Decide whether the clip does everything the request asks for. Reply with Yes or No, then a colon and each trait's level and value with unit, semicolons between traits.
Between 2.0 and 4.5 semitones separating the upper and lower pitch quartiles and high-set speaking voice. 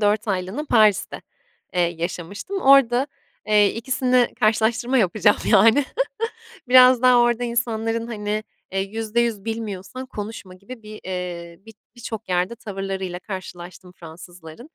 Yes: average, 4.1 semitones; high, 215 Hz